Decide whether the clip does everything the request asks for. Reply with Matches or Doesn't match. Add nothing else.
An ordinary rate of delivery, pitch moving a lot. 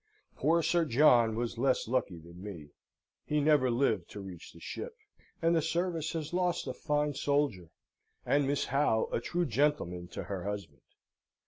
Matches